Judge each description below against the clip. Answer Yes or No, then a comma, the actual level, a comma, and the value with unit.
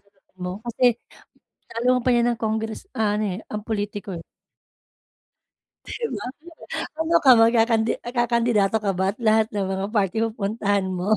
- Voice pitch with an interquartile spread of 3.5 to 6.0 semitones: No, narrow, 2.6 semitones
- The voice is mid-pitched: No, high, 220 Hz